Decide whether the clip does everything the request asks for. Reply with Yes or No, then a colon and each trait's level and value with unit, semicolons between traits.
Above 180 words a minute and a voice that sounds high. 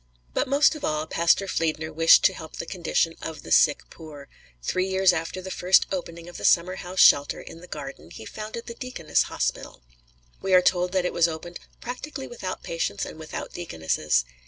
No: average, 190 wpm; medium, 175 Hz